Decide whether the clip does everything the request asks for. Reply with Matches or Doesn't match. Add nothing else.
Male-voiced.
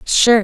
Doesn't match